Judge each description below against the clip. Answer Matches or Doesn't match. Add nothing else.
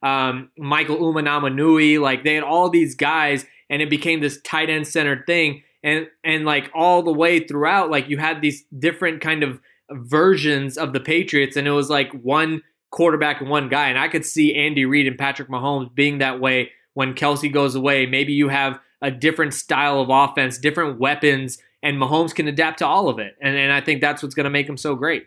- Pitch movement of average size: Doesn't match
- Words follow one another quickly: Matches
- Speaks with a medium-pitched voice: Matches